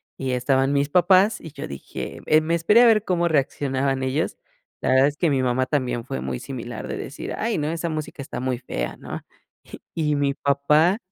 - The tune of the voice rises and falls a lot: No, average, 4.1 semitones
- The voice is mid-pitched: Yes, medium, 145 Hz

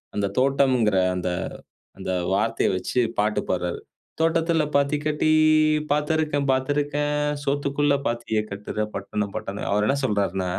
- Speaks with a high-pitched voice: No, low, 130 Hz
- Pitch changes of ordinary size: No, wide, 6.3 semitones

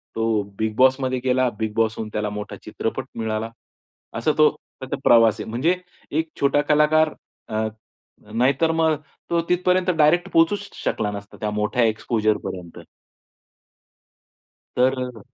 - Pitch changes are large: Yes, wide, 5.8 semitones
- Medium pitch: No, low, 125 Hz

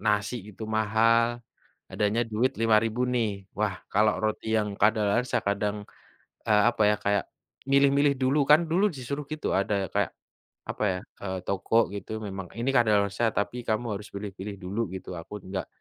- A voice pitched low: Yes, low, 110 Hz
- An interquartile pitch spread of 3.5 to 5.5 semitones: No, average, 2.9 semitones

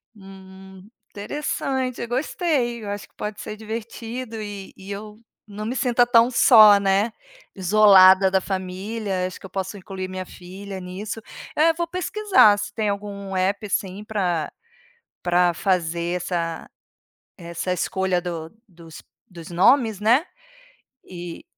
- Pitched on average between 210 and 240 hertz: No, high, 200 Hz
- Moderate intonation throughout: Yes, average, 3.1 semitones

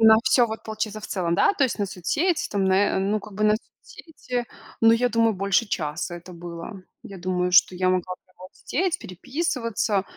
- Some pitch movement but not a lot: Yes, average, 4.0 semitones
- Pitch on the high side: Yes, high, 205 Hz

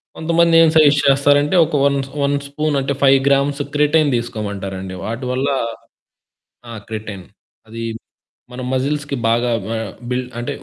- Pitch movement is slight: No, average, 3.9 semitones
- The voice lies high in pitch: No, medium, 140 Hz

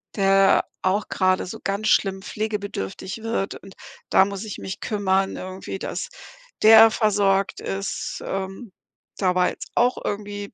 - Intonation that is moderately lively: No, narrow, 1.7 semitones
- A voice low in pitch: No, high, 195 Hz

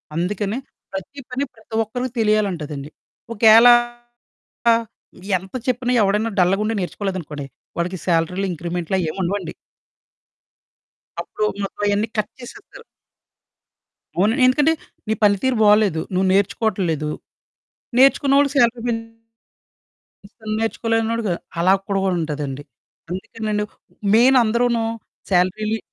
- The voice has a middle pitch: No, high, 210 Hz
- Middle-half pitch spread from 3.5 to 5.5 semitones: Yes, average, 4.0 semitones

